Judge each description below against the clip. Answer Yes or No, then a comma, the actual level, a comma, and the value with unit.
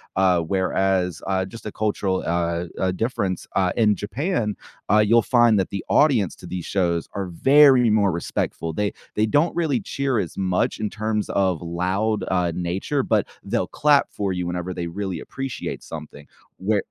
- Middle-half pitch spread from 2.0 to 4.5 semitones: Yes, average, 3.6 semitones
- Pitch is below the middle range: Yes, low, 100 Hz